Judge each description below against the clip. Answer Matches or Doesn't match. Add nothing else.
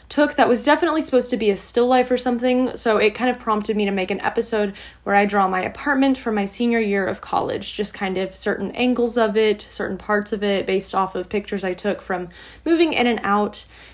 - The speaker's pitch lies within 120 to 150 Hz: Doesn't match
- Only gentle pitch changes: Doesn't match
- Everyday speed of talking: Doesn't match